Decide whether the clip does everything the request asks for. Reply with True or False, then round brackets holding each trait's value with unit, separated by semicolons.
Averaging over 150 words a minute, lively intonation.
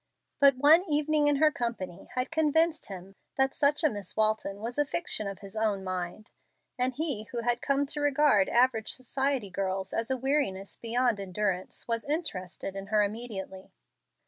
True (170 wpm; 6.3 semitones)